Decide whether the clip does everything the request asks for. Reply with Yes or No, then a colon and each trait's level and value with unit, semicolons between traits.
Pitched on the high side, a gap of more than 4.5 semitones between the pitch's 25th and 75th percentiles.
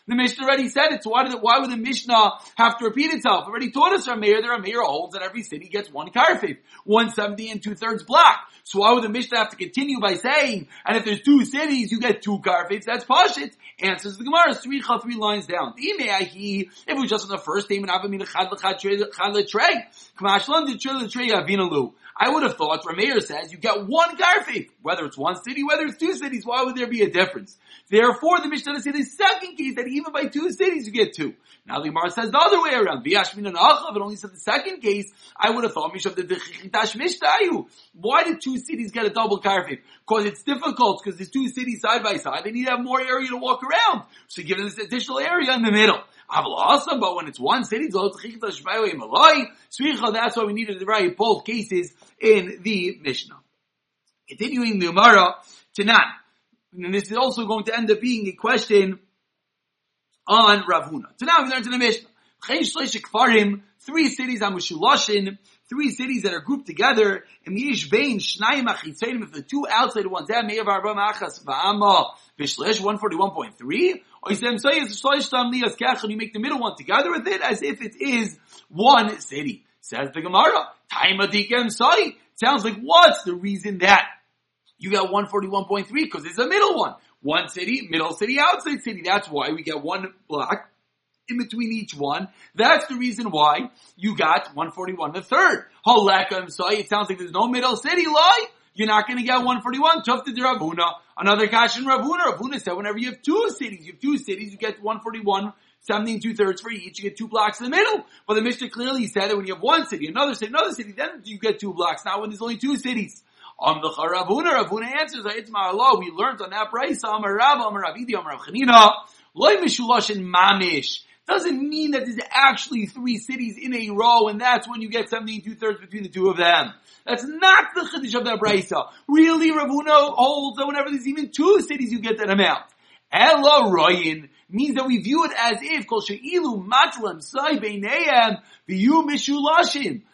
Yes: high, 230 Hz; average, 5.1 semitones